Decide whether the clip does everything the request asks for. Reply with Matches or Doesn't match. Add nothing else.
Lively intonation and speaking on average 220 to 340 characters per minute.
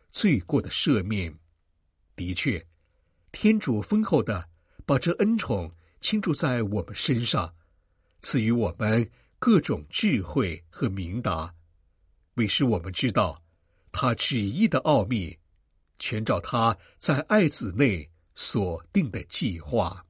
Doesn't match